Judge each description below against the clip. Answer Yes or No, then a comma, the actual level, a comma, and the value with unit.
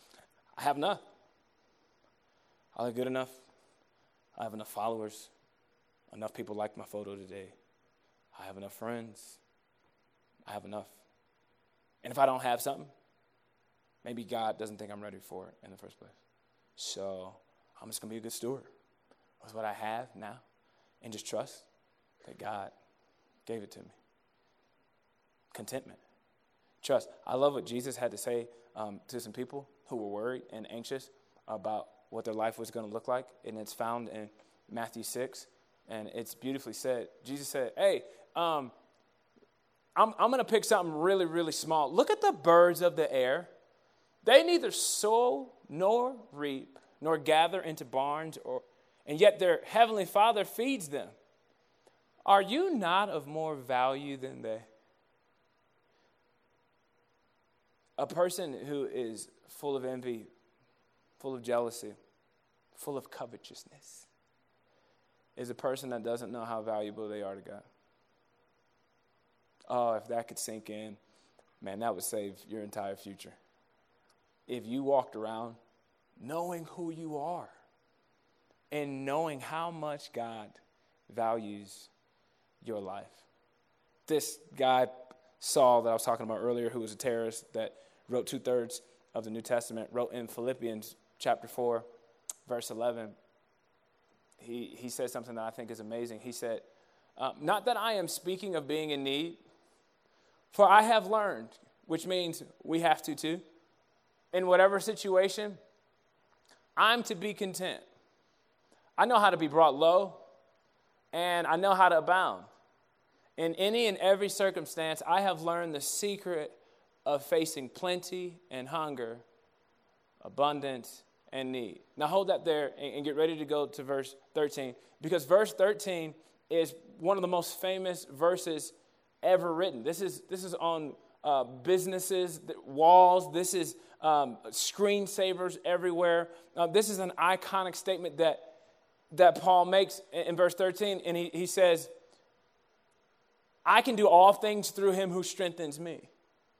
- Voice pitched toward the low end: No, medium, 150 Hz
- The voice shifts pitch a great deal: Yes, wide, 7.5 semitones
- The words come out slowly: No, average, 150 wpm